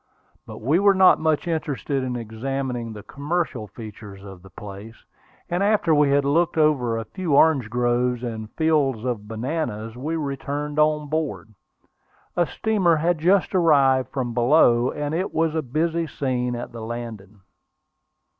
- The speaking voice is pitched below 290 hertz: Yes, low, 135 Hz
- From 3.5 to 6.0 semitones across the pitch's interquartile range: Yes, wide, 5.4 semitones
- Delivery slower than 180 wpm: Yes, average, 155 wpm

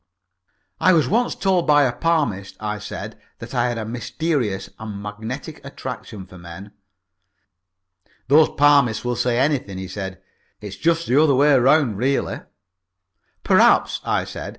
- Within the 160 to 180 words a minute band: No, average, 150 wpm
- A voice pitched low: Yes, low, 125 Hz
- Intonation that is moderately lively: No, wide, 6.0 semitones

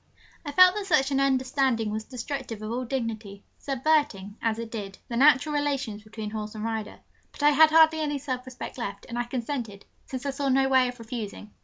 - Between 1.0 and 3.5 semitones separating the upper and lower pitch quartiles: No, average, 4.2 semitones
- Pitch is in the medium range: No, very high, 255 Hz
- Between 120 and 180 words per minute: No, fast, 205 wpm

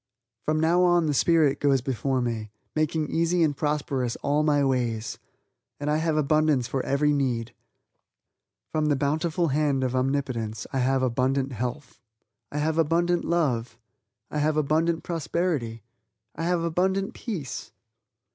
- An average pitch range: Yes, average, 3.7 semitones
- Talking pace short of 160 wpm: Yes, average, 145 wpm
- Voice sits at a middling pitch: Yes, medium, 145 Hz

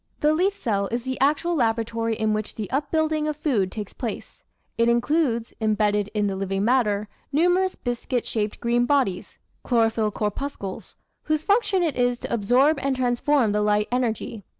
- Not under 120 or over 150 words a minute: No, average, 165 wpm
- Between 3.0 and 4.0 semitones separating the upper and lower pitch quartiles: No, average, 5.2 semitones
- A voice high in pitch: Yes, high, 240 Hz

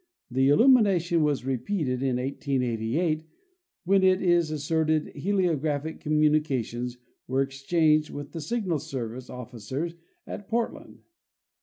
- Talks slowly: Yes, slow, 120 wpm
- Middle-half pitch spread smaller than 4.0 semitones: No, average, 4.4 semitones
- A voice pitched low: No, medium, 150 Hz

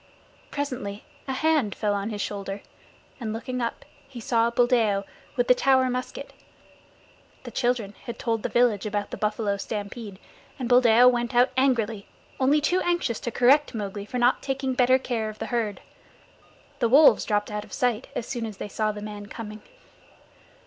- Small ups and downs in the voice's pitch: No, average, 3.2 semitones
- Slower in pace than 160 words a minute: No, average, 175 wpm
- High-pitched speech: Yes, high, 235 Hz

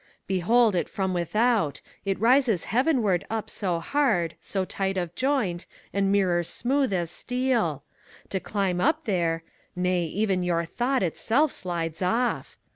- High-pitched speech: Yes, high, 195 Hz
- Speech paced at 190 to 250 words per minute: No, average, 150 wpm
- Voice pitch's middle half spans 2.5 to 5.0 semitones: No, wide, 5.5 semitones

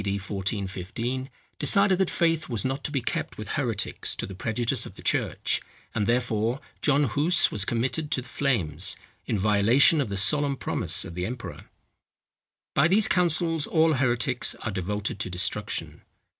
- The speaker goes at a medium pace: Yes, average, 165 wpm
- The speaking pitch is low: Yes, low, 120 Hz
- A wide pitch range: Yes, wide, 6.4 semitones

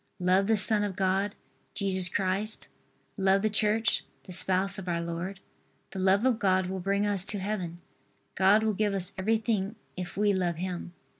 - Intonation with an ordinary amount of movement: No, narrow, 2.0 semitones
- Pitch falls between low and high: No, high, 195 Hz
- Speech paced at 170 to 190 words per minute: Yes, average, 175 wpm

